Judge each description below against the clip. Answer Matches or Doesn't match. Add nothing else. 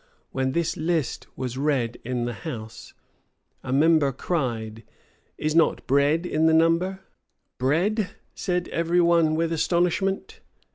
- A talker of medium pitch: Matches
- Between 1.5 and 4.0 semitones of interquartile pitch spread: Doesn't match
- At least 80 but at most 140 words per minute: Matches